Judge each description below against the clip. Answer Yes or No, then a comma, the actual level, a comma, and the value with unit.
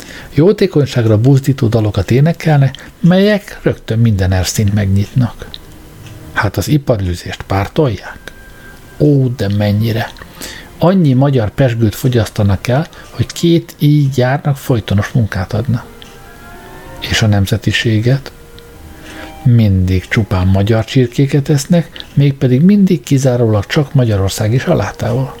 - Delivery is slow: Yes, slow, 100 wpm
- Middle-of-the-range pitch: No, low, 120 Hz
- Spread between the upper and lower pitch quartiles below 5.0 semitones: No, wide, 5.6 semitones